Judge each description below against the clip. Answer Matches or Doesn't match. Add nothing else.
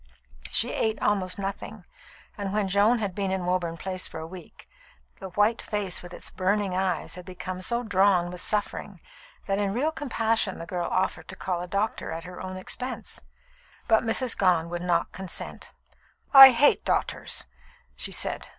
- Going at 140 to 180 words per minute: Matches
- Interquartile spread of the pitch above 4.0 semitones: Doesn't match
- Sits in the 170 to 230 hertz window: Matches